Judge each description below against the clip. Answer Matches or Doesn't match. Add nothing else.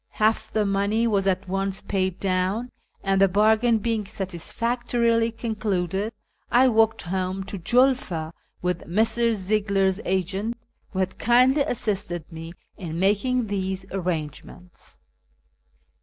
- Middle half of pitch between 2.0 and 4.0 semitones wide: Matches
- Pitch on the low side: Doesn't match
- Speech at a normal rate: Doesn't match